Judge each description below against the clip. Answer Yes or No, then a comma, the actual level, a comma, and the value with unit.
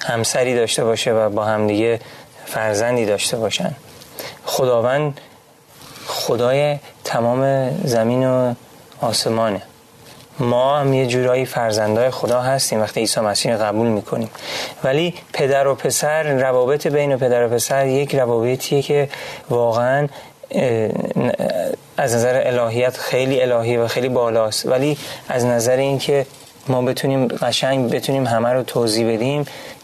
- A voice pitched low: Yes, low, 125 Hz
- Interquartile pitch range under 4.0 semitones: Yes, average, 2.8 semitones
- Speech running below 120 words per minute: No, average, 125 wpm